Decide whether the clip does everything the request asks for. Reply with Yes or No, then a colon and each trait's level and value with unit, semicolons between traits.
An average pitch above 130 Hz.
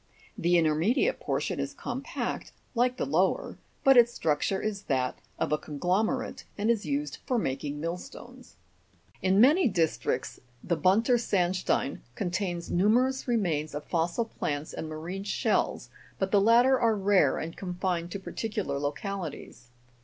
Yes: high, 190 Hz